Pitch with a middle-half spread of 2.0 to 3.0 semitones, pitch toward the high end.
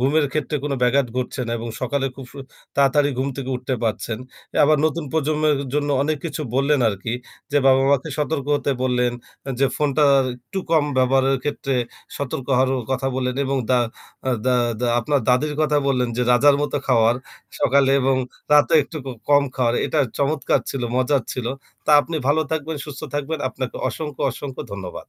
No: narrow, 2.5 semitones; low, 135 Hz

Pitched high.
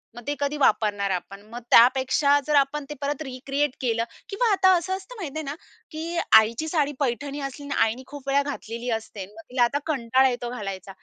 Yes: very high, 275 Hz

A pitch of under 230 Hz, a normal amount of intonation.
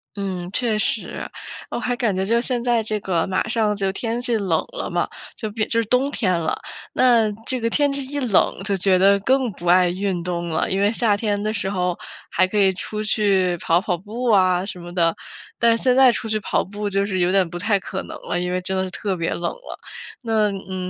Yes: high, 200 Hz; average, 3.7 semitones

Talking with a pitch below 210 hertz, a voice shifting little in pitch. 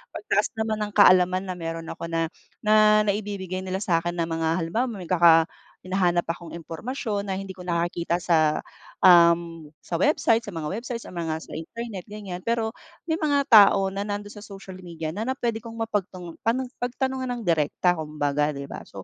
No: medium, 185 Hz; average, 4.3 semitones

